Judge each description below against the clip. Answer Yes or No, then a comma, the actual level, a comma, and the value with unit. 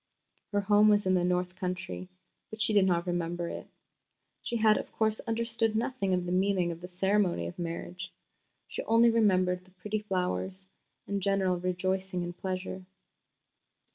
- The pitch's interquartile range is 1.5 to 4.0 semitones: Yes, narrow, 2.6 semitones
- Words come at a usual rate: Yes, average, 165 wpm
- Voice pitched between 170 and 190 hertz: Yes, medium, 185 Hz